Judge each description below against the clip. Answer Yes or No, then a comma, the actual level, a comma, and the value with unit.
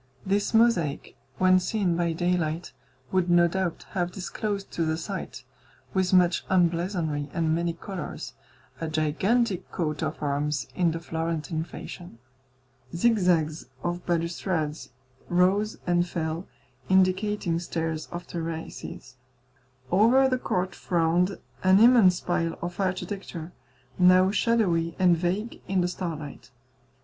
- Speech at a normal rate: No, slow, 120 wpm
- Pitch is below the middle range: No, medium, 175 Hz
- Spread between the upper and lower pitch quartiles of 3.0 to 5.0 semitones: No, narrow, 2.4 semitones